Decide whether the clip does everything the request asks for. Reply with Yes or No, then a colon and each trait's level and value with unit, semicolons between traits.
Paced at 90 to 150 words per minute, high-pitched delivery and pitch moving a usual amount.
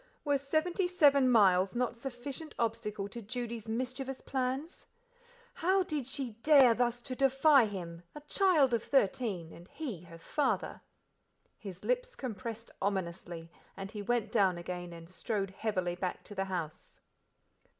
No: average, 145 wpm; high, 235 Hz; wide, 6.1 semitones